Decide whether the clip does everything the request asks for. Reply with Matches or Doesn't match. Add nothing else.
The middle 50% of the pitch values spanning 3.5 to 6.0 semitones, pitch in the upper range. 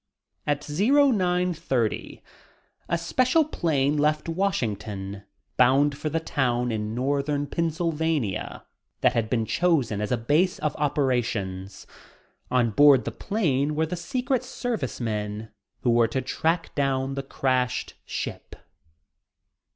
Doesn't match